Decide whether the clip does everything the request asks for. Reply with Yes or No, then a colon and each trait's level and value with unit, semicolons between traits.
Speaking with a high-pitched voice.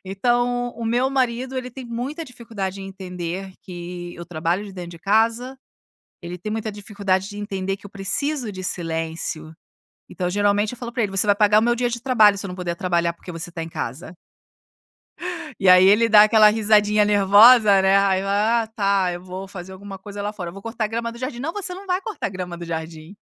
Yes: high, 200 Hz